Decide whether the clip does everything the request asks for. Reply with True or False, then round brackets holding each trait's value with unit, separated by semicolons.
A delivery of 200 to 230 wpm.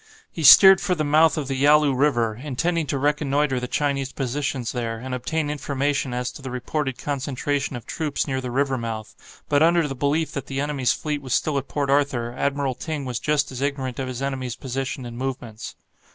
True (205 wpm)